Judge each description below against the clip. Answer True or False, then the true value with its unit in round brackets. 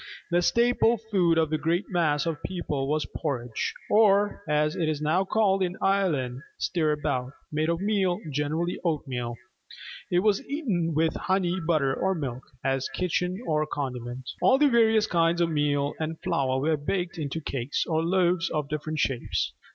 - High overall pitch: False (165 Hz)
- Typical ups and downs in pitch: True (4.3 semitones)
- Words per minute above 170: False (165 wpm)